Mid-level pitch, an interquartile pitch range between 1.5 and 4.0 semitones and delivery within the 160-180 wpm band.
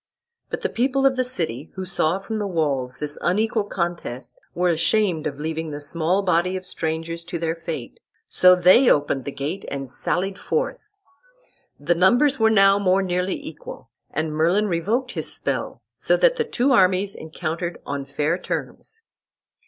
No: medium, 180 Hz; average, 4.5 semitones; average, 170 wpm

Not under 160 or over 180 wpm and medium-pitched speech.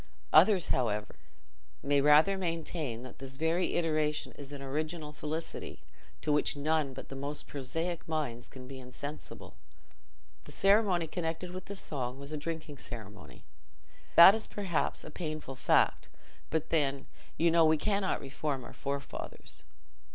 No: average, 145 wpm; medium, 150 Hz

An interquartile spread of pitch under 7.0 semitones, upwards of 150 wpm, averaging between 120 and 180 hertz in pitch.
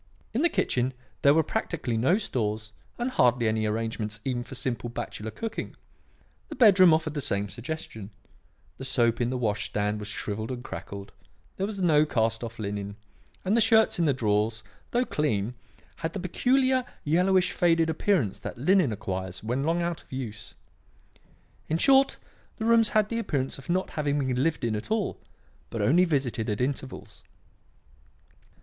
No: wide, 8.3 semitones; average, 170 wpm; low, 135 Hz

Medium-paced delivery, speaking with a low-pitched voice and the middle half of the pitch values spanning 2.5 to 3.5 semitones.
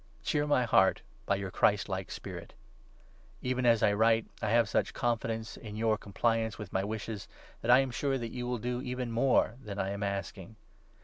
Yes: average, 195 wpm; low, 115 Hz; average, 3.2 semitones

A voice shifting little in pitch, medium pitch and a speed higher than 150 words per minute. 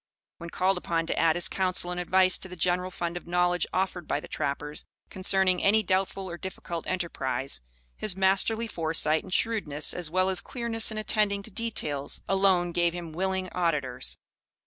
Yes: narrow, 2.3 semitones; medium, 180 Hz; average, 175 wpm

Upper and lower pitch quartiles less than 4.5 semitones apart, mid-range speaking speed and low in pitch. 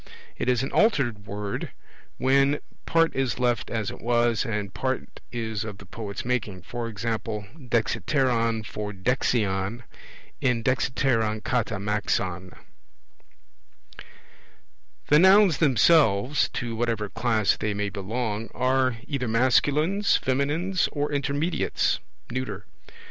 No: average, 4.0 semitones; slow, 110 wpm; low, 120 Hz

